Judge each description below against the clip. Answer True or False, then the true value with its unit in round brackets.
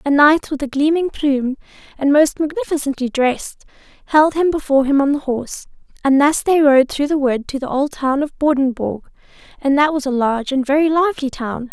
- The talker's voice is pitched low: False (280 Hz)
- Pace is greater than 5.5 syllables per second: True (5.7 syllables/s)